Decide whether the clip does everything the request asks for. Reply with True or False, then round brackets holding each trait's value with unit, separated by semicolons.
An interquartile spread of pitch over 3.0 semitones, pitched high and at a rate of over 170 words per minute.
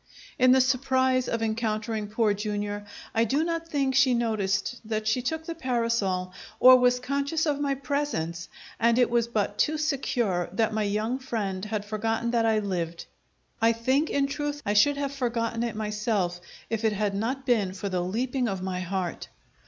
True (4.0 semitones; 230 Hz; 185 wpm)